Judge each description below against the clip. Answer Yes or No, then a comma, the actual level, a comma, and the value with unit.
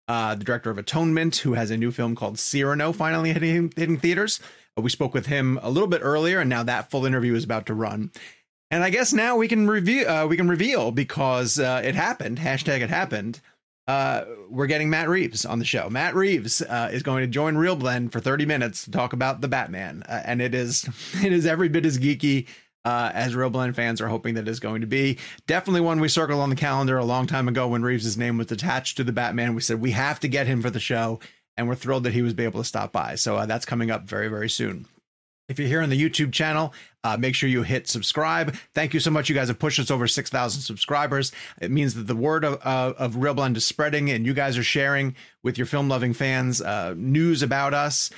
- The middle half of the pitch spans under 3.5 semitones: No, average, 4.0 semitones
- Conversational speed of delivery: No, fast, 245 wpm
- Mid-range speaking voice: No, low, 130 Hz